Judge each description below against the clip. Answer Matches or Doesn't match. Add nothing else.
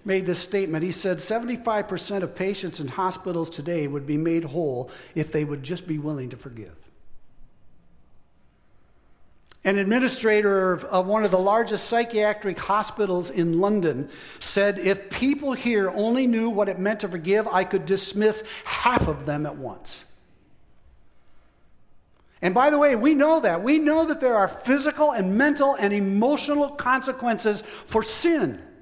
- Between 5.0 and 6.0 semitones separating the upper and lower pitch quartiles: Matches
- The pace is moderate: Matches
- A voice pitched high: Matches